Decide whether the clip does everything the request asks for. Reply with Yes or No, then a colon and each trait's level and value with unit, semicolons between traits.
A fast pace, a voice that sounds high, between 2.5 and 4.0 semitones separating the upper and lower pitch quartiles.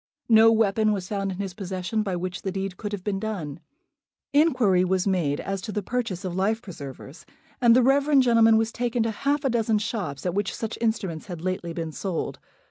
Yes: fast, 210 wpm; high, 200 Hz; average, 3.6 semitones